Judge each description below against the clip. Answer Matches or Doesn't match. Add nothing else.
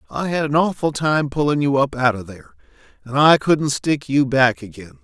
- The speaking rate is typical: Doesn't match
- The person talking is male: Matches